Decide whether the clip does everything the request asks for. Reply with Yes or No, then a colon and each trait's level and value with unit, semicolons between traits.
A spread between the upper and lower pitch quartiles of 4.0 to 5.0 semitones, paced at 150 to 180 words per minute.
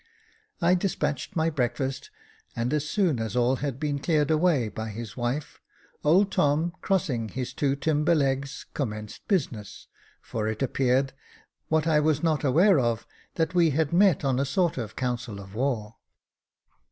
Yes: average, 4.6 semitones; average, 160 wpm